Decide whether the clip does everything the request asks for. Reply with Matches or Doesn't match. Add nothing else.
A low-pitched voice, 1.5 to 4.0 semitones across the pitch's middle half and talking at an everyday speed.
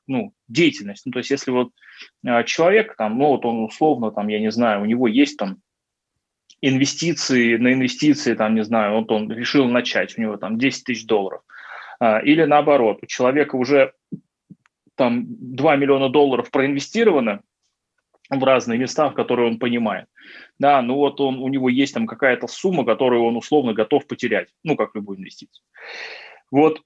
Doesn't match